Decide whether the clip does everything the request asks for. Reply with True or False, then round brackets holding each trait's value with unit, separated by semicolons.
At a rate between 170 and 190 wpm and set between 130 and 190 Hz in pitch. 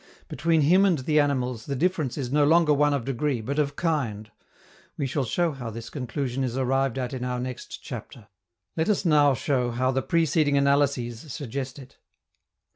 True (185 wpm; 140 Hz)